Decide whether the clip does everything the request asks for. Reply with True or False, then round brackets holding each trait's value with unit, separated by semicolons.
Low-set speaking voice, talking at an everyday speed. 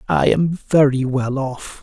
True (130 Hz; 165 wpm)